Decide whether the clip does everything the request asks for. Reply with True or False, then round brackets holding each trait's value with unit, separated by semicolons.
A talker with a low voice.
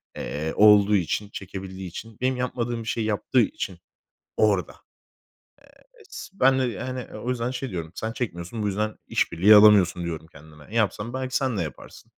True (105 Hz)